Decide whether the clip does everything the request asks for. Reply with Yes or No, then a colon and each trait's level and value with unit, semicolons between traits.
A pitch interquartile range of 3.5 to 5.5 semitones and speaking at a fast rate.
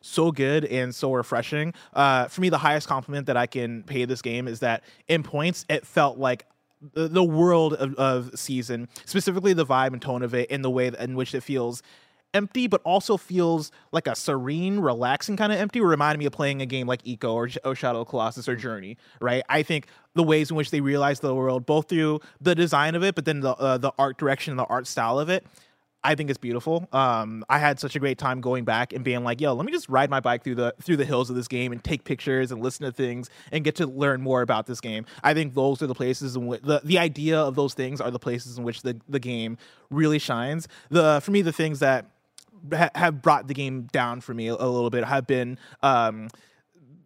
Yes: average, 3.8 semitones; fast, 240 wpm